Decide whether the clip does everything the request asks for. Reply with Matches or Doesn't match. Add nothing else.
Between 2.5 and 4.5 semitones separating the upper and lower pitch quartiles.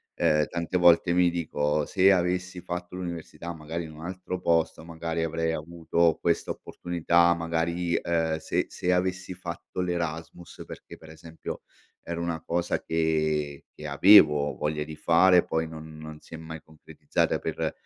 Doesn't match